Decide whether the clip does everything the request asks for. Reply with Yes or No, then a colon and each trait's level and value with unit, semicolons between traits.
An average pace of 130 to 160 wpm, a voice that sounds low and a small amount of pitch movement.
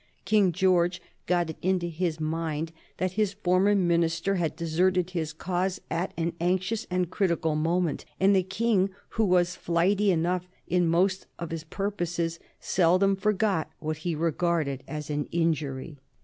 No: average, 150 wpm; medium, 175 Hz; narrow, 2.3 semitones